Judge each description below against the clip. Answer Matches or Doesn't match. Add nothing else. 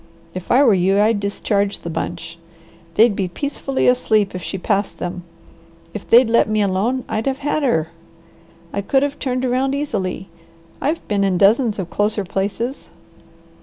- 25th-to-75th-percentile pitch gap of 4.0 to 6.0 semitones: Matches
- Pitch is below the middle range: Doesn't match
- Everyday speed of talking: Matches